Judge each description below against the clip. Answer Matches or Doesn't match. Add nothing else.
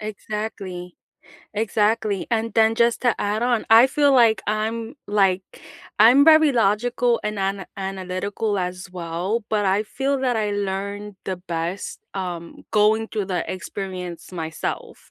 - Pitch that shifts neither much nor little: Matches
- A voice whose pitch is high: Matches